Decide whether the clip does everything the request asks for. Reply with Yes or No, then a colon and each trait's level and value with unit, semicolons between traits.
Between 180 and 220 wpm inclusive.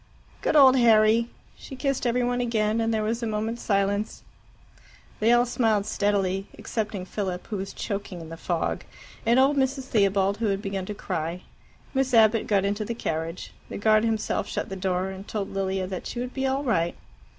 Yes: average, 195 wpm